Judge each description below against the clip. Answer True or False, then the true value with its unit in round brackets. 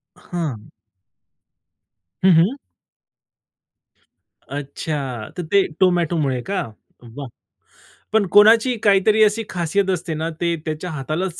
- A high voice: False (175 Hz)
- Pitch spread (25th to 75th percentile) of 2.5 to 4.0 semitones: False (4.7 semitones)